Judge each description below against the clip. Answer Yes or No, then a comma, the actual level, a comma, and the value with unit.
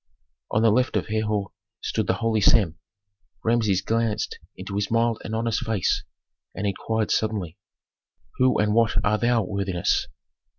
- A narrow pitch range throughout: Yes, narrow, 2.2 semitones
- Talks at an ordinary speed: Yes, average, 145 wpm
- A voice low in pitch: Yes, low, 110 Hz